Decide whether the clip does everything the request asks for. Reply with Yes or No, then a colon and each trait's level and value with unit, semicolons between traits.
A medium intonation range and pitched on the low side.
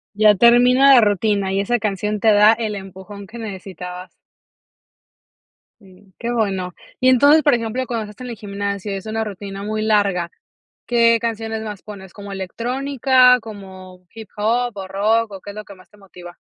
No: average, 3.0 semitones; high, 210 Hz